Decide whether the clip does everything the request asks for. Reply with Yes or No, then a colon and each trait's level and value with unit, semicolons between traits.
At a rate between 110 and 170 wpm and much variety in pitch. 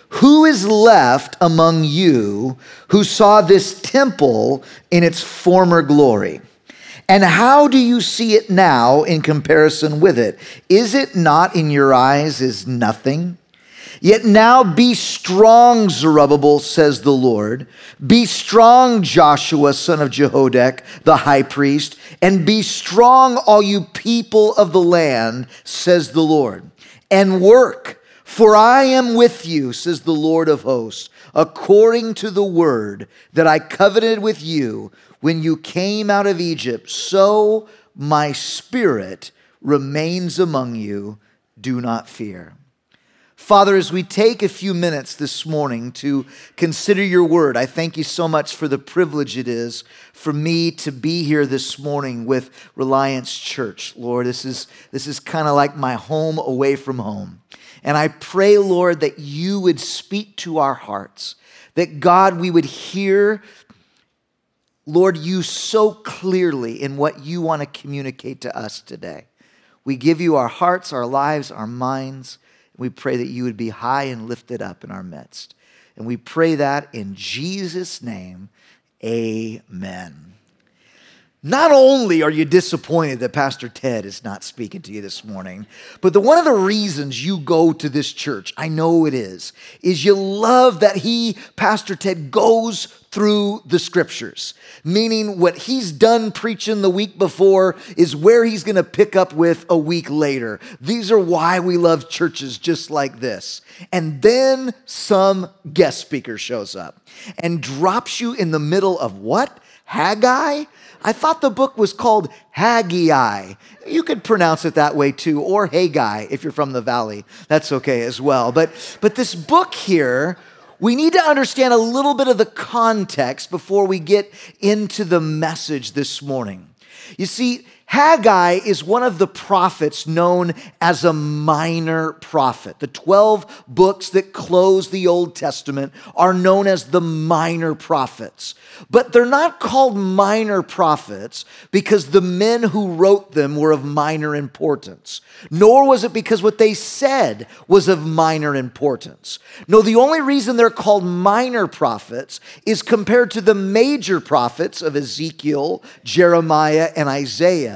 Yes: average, 155 wpm; wide, 6.3 semitones